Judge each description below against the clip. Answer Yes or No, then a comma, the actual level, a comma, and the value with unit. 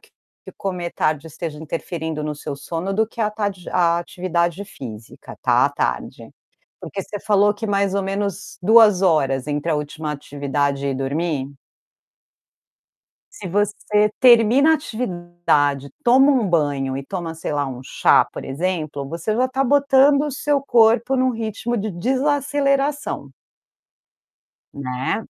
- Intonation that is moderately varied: No, wide, 7.1 semitones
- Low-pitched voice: No, medium, 185 Hz